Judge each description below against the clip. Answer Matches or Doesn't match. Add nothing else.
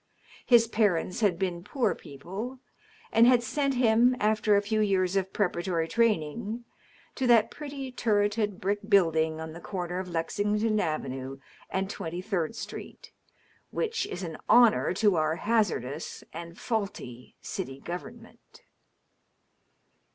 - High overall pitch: Matches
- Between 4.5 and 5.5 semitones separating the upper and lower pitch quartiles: Matches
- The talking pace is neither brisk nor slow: Doesn't match